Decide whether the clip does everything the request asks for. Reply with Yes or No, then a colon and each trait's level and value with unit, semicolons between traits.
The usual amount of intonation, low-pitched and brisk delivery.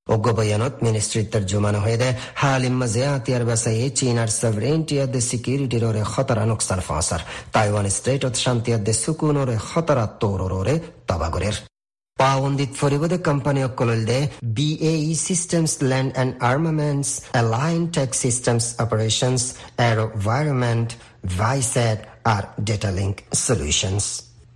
Yes: average, 3.6 semitones; low, 120 Hz; fast, 125 wpm